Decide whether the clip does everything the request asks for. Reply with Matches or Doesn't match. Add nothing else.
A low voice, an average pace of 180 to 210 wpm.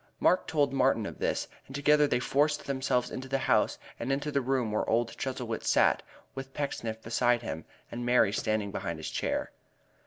Matches